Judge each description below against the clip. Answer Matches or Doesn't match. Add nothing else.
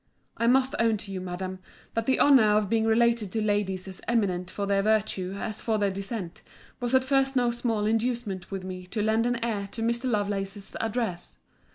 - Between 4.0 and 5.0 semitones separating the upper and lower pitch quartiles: Doesn't match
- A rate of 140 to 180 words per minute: Doesn't match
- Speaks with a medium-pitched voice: Doesn't match